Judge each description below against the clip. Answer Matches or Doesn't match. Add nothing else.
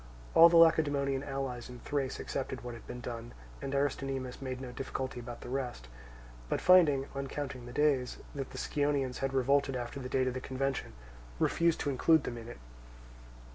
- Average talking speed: Matches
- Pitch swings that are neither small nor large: Doesn't match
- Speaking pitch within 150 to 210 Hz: Doesn't match